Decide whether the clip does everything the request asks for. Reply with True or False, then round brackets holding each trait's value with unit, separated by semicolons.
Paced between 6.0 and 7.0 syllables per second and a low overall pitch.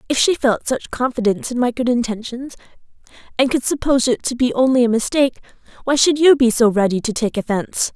False (6.1 syllables/s; 245 Hz)